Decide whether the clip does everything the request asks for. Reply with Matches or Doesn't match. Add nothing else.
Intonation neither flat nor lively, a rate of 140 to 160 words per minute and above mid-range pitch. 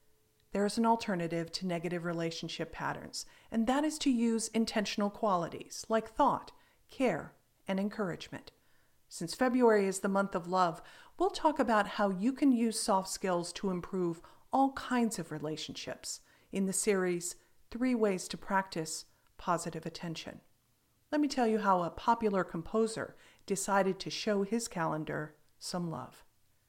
Matches